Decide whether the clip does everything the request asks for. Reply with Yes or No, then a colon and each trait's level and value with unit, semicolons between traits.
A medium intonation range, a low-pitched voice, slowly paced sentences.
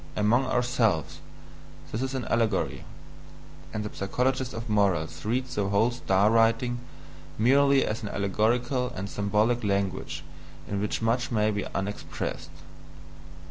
Yes: average, 3.3 semitones; low, 110 Hz; slow, 130 wpm